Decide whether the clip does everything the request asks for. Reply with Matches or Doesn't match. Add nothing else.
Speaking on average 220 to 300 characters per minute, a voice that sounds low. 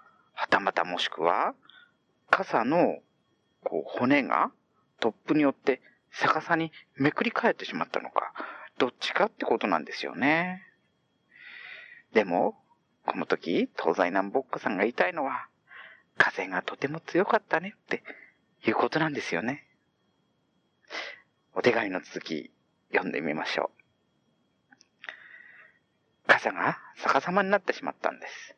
Doesn't match